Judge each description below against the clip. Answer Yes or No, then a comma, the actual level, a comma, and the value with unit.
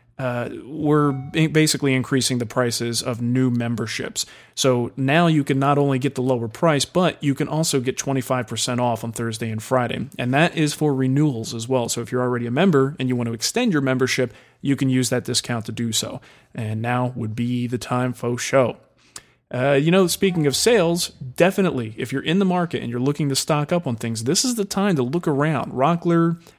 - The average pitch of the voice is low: Yes, low, 130 Hz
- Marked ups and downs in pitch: No, average, 3.7 semitones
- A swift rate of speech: Yes, fast, 215 wpm